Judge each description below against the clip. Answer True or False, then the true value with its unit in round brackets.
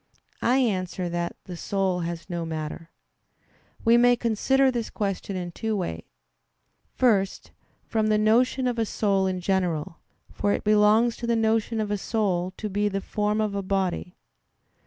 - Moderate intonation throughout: True (3.5 semitones)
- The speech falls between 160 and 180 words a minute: True (165 wpm)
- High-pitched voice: True (205 Hz)